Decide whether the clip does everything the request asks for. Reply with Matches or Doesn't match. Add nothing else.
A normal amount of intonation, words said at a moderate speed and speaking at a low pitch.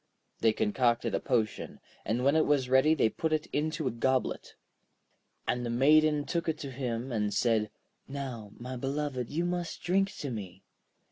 Matches